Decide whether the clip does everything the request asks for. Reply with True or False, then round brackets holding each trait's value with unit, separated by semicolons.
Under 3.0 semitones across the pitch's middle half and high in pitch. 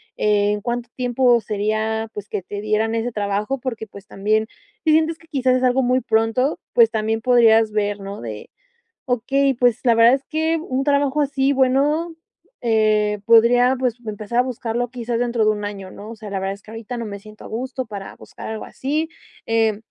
False (3.3 semitones; 230 Hz)